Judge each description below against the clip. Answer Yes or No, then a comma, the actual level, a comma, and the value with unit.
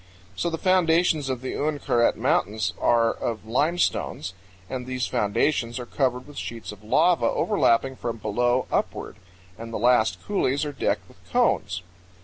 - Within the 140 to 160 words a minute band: Yes, average, 150 wpm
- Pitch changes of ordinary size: Yes, average, 4.4 semitones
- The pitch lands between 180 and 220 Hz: No, low, 125 Hz